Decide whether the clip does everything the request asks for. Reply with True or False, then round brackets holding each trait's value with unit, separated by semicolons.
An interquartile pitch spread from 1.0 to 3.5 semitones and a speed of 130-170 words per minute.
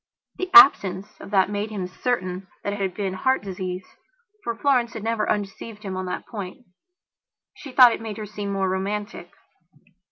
False (3.1 semitones; 180 wpm)